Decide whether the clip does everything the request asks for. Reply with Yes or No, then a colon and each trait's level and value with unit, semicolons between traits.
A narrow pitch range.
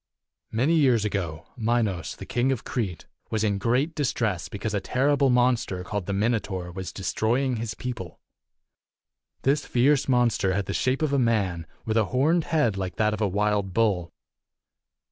No: average, 4.5 semitones